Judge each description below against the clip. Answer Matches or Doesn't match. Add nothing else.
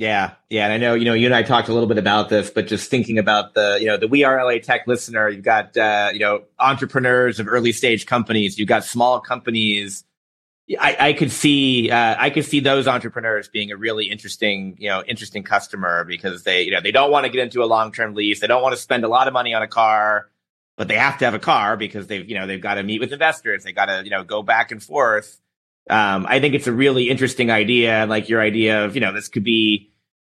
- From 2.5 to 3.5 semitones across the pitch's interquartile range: Matches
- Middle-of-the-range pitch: Doesn't match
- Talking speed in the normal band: Doesn't match